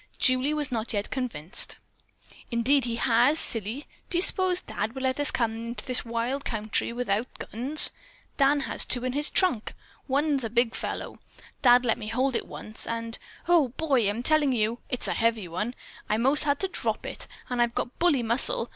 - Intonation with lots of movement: No, average, 3.6 semitones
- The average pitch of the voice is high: Yes, high, 245 Hz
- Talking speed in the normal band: Yes, average, 190 wpm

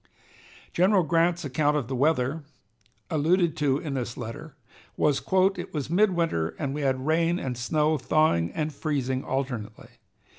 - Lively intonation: No, average, 3.9 semitones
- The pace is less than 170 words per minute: Yes, average, 145 wpm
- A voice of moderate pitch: Yes, medium, 150 Hz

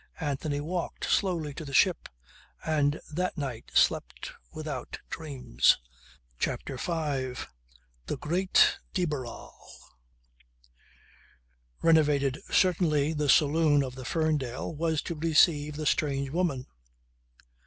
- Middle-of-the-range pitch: Yes, medium, 150 Hz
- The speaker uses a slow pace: Yes, slow, 105 wpm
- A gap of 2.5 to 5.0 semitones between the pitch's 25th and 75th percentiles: Yes, average, 2.8 semitones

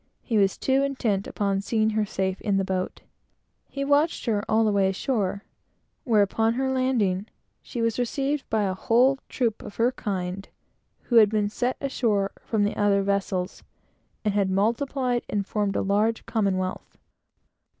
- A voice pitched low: No, high, 210 Hz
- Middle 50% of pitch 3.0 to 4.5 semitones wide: Yes, average, 3.7 semitones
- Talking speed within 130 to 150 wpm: No, average, 165 wpm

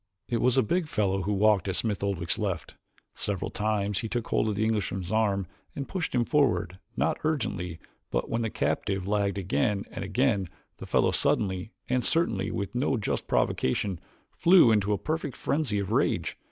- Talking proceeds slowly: No, average, 180 wpm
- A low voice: Yes, low, 105 Hz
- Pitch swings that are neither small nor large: Yes, average, 3.8 semitones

